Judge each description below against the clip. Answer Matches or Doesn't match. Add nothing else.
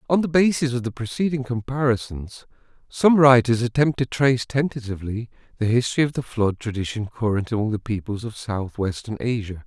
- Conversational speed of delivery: Matches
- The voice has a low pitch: Matches